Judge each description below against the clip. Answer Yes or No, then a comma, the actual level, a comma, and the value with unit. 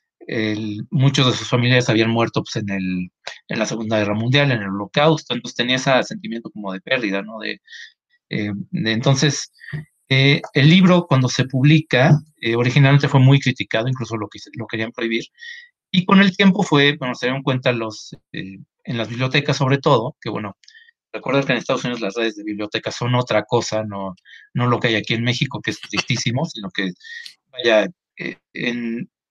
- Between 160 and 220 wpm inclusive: Yes, fast, 190 wpm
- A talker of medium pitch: No, low, 125 Hz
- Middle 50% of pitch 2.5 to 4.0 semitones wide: No, average, 4.8 semitones